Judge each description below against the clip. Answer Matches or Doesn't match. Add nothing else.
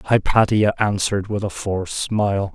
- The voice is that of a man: Matches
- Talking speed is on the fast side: Doesn't match